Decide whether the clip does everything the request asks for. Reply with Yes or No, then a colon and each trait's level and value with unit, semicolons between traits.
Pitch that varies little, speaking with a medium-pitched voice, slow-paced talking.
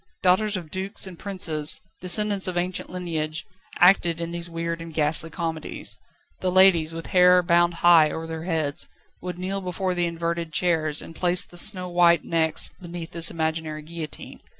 No: narrow, 2.0 semitones; medium, 170 Hz; average, 165 wpm